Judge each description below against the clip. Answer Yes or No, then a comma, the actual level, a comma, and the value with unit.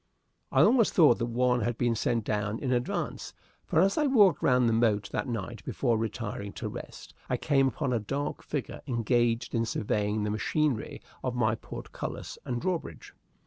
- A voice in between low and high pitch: No, low, 120 Hz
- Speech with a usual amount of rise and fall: Yes, average, 3.4 semitones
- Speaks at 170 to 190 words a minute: Yes, average, 180 wpm